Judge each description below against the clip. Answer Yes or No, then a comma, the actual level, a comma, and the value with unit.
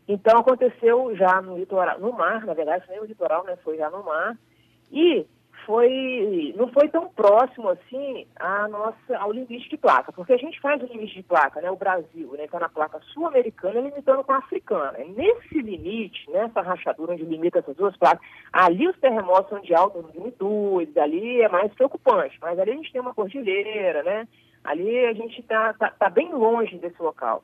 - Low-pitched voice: No, high, 225 Hz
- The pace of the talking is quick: Yes, fast, 195 wpm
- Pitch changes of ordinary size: No, wide, 6.8 semitones